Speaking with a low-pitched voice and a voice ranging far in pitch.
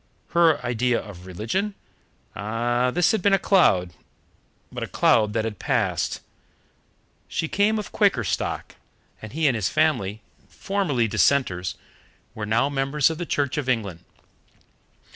Yes: low, 125 Hz; wide, 7.1 semitones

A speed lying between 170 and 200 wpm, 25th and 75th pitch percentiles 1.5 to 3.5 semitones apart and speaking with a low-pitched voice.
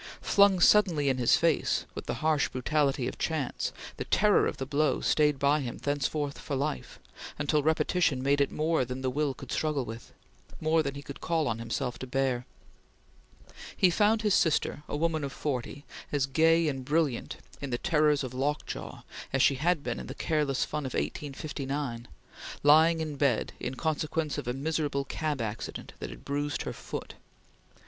No: average, 180 wpm; average, 2.9 semitones; medium, 145 Hz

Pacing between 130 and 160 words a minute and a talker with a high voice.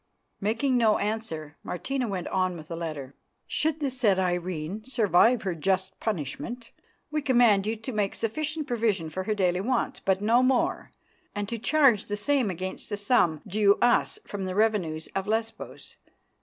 No: average, 170 wpm; high, 210 Hz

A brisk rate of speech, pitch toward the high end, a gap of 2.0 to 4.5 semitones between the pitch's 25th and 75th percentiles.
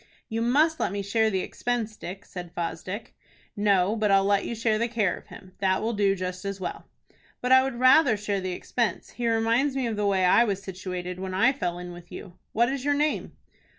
Yes: fast, 225 wpm; high, 205 Hz; average, 4.1 semitones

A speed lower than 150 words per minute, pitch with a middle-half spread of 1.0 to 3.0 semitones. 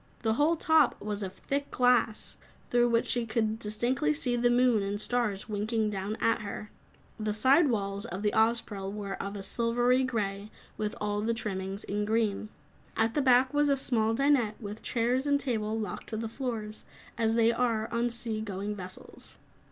No: average, 180 wpm; average, 2.7 semitones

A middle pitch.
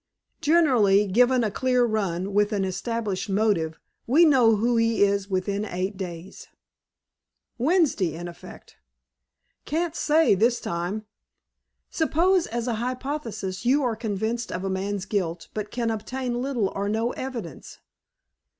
No: high, 220 Hz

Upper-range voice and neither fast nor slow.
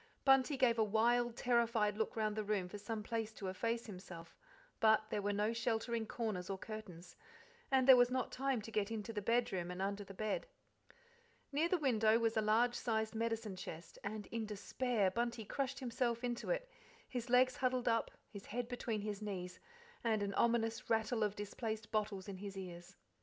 Yes: high, 220 Hz; average, 190 wpm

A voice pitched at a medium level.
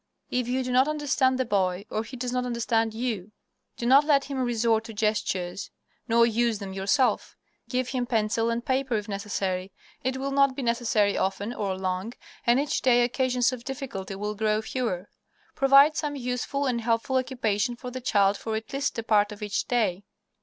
No: high, 235 Hz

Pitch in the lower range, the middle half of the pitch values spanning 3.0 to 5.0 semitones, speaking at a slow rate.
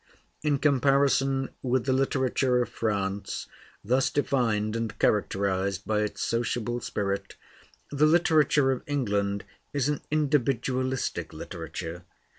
Yes: low, 125 Hz; average, 4.7 semitones; slow, 110 wpm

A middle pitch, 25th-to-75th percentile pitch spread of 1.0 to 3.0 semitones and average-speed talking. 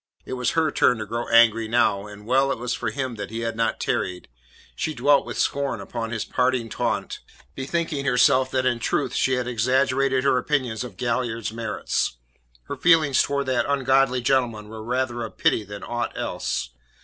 No: low, 125 Hz; average, 2.7 semitones; average, 185 wpm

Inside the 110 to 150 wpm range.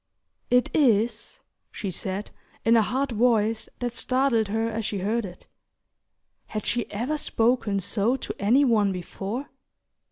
Yes: average, 140 wpm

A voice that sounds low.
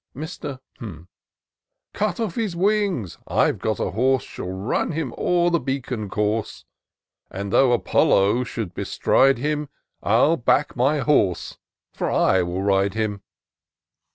Yes: low, 125 Hz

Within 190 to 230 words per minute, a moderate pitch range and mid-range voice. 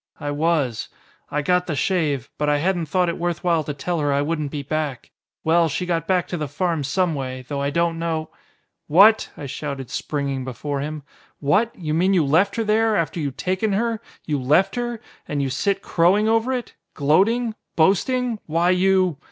Yes: average, 200 wpm; average, 4.7 semitones; medium, 165 Hz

